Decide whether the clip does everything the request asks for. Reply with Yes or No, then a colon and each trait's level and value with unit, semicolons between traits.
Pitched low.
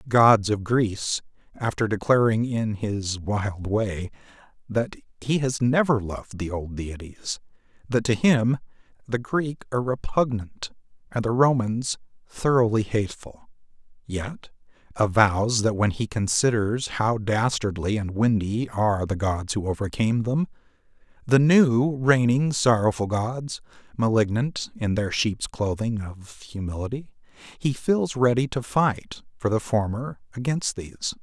Yes: low, 115 Hz